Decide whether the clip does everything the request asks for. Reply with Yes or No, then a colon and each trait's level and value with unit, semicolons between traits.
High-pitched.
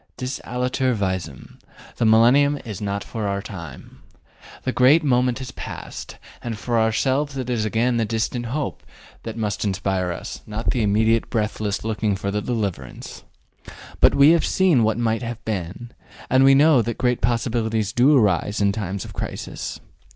No: low, 115 Hz